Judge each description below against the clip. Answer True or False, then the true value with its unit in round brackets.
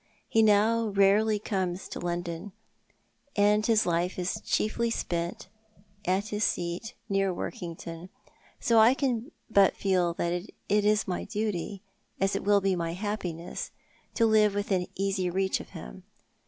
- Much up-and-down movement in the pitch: False (3.1 semitones)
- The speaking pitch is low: False (195 Hz)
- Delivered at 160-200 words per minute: False (145 wpm)